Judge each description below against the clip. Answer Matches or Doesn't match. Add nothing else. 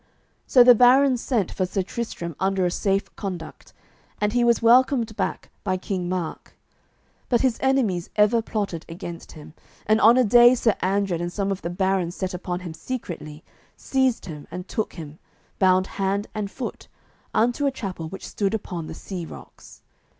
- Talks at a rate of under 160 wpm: Doesn't match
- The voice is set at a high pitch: Matches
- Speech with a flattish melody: Doesn't match